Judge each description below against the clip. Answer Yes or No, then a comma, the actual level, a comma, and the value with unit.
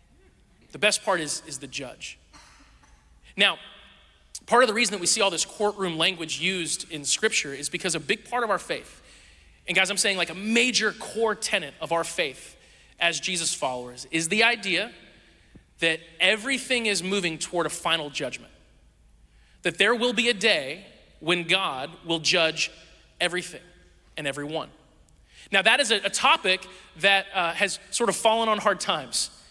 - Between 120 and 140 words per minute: No, average, 170 wpm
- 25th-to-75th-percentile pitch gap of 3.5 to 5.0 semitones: Yes, average, 4.5 semitones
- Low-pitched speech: No, medium, 180 Hz